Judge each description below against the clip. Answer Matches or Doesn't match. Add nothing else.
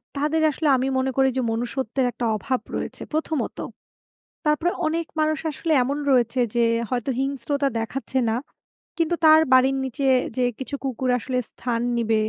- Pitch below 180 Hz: Doesn't match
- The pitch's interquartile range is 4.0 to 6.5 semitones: Doesn't match